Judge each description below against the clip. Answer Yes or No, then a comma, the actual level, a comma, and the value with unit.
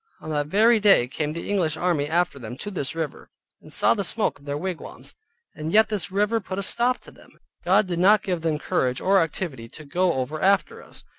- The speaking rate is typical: No, fast, 225 wpm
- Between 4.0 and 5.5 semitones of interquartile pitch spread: Yes, average, 4.9 semitones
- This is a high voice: No, medium, 175 Hz